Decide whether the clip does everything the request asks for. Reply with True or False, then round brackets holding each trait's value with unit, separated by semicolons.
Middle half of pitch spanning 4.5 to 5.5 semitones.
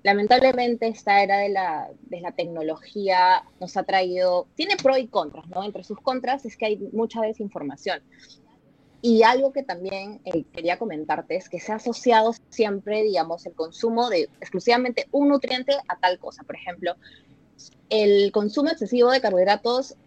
True (4.8 semitones)